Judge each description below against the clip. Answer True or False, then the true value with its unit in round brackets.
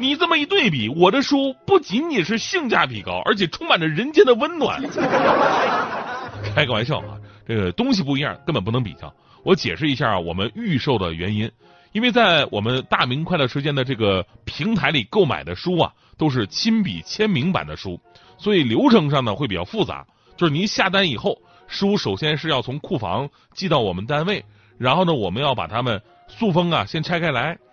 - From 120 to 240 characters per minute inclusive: False (295 characters per minute)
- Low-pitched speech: False (150 Hz)